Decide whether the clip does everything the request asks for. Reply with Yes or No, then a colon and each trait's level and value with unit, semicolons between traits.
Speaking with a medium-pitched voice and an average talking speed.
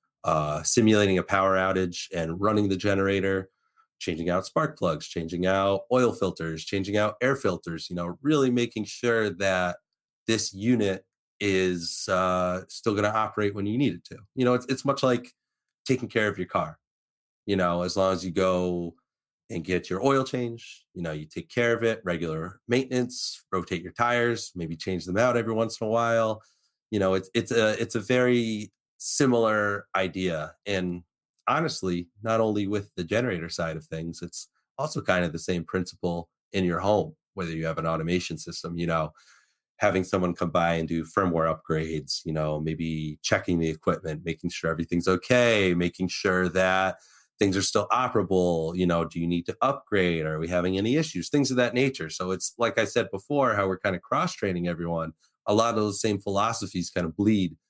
No: very low, 95 Hz; average, 190 wpm